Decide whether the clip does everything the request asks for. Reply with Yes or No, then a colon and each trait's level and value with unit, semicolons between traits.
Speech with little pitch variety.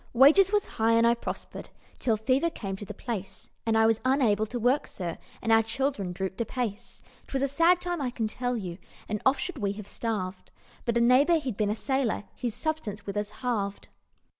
No: average, 4.3 semitones